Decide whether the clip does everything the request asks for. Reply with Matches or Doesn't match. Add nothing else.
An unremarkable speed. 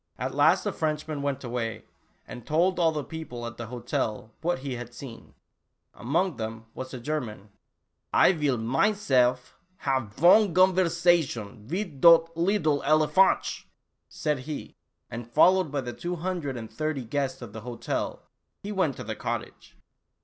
Matches